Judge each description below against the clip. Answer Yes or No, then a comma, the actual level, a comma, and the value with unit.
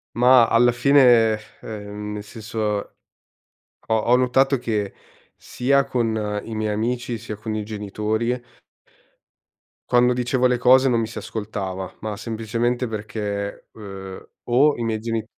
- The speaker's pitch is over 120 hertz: No, low, 115 Hz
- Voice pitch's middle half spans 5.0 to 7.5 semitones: No, average, 2.7 semitones